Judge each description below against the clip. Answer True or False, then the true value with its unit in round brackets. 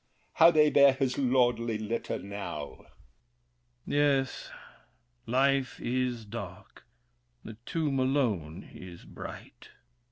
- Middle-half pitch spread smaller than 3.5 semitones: False (4.4 semitones)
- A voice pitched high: False (125 Hz)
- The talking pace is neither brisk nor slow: False (105 wpm)